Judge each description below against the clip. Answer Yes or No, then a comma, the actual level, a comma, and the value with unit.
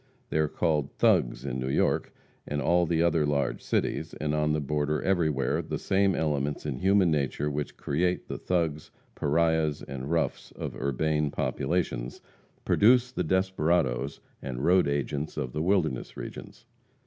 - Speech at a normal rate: Yes, average, 160 wpm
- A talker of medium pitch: No, very low, 75 Hz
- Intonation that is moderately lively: Yes, average, 3.2 semitones